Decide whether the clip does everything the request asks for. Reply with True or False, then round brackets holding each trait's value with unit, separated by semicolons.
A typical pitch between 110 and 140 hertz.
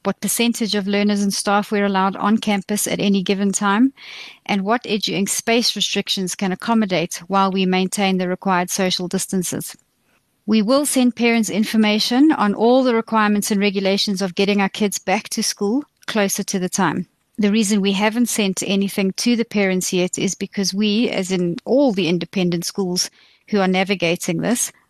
False (200 Hz)